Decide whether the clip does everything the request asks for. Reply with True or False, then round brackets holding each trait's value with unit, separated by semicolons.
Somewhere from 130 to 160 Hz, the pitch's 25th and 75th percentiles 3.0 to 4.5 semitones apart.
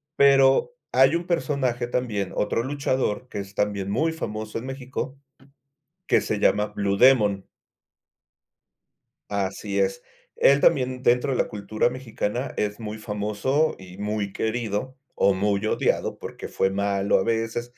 False (110 Hz; 4.2 semitones)